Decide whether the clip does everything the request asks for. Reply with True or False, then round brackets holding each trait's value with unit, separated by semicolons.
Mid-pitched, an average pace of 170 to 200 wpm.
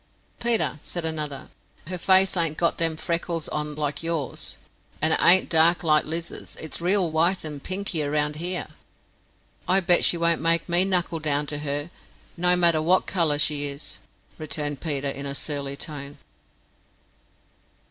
False (160 Hz; 155 wpm)